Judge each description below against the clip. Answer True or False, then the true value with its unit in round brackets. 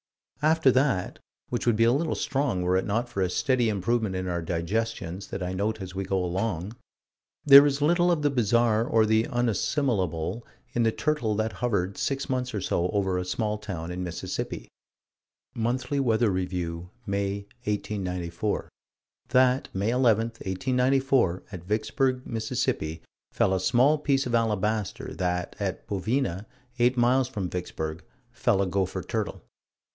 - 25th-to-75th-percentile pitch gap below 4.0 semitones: False (5.2 semitones)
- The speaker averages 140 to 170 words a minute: True (155 wpm)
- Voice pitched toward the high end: False (110 Hz)